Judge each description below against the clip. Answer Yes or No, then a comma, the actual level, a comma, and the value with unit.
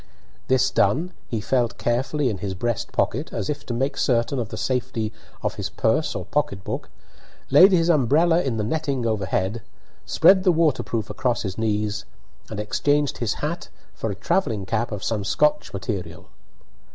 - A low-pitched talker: Yes, low, 120 Hz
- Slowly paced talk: No, average, 170 wpm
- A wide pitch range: Yes, wide, 5.7 semitones